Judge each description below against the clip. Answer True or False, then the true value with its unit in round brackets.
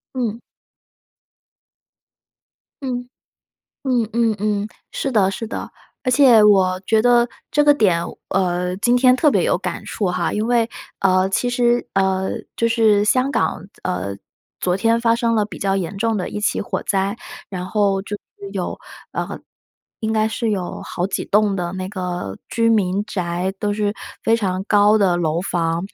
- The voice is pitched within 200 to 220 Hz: True (205 Hz)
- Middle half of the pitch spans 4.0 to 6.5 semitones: False (3.6 semitones)